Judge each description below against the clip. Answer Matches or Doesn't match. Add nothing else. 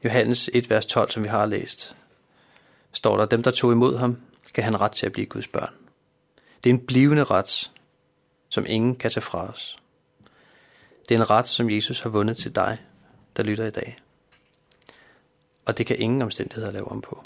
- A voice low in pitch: Matches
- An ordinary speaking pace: Matches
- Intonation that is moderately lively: Doesn't match